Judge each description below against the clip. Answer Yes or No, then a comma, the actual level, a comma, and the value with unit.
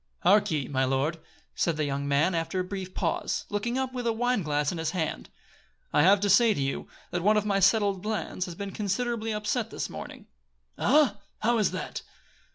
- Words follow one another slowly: No, fast, 205 wpm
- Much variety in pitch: No, average, 5.0 semitones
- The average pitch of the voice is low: No, high, 195 Hz